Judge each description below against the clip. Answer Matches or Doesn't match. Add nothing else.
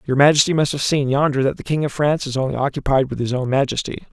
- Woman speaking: Doesn't match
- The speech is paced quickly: Matches